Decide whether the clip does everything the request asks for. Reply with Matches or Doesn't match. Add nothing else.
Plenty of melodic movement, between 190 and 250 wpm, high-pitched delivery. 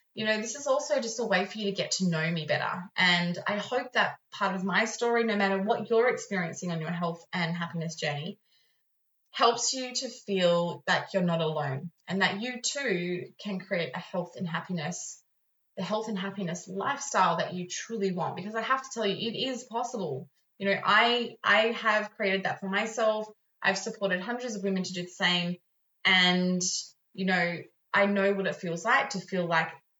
Doesn't match